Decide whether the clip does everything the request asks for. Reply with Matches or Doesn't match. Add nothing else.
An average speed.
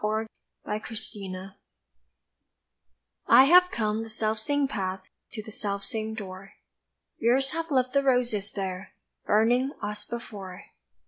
Doesn't match